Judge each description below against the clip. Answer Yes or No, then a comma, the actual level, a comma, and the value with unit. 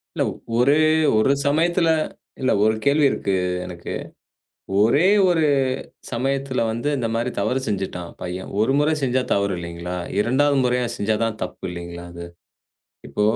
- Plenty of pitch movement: Yes, wide, 6.1 semitones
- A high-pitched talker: No, low, 115 Hz